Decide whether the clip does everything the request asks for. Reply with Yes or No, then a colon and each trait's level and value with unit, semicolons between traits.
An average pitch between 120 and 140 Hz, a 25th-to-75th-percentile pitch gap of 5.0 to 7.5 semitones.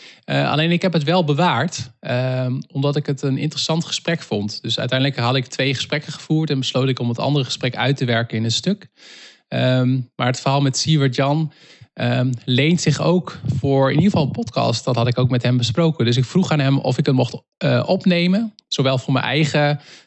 No: low, 135 Hz; average, 3.8 semitones